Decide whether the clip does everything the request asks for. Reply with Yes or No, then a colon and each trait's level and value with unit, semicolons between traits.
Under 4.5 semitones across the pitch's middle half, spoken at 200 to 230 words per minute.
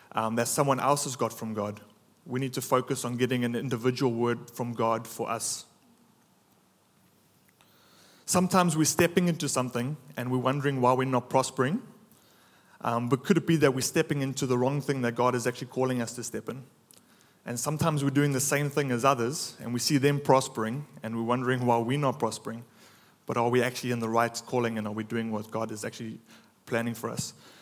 Yes: average, 3.3 semitones; fast, 205 wpm